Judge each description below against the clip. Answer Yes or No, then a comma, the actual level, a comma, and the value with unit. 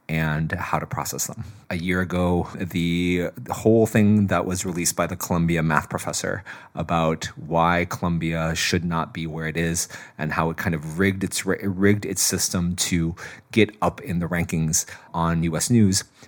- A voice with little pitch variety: Yes, narrow, 2.3 semitones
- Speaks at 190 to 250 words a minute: No, average, 175 wpm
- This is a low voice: Yes, very low, 85 Hz